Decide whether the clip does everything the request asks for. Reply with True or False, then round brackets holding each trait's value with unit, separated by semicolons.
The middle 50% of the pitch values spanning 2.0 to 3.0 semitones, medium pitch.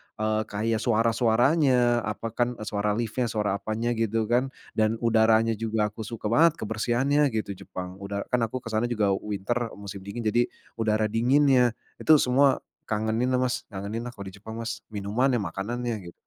False (2.4 semitones; 115 Hz)